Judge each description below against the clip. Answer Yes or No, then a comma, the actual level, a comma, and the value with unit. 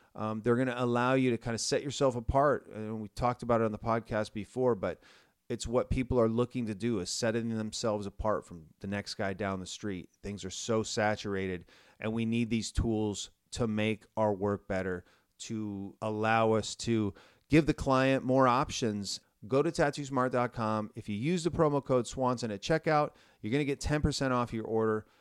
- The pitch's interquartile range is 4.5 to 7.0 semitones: No, average, 3.2 semitones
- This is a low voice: Yes, low, 110 Hz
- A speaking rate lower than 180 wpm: No, average, 200 wpm